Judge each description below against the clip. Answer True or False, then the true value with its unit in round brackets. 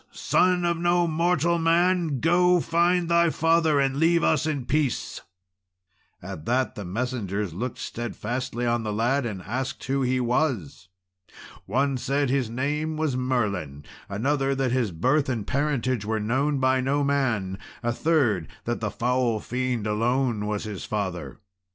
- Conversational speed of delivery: True (150 wpm)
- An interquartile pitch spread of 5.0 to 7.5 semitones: True (5.3 semitones)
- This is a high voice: False (130 Hz)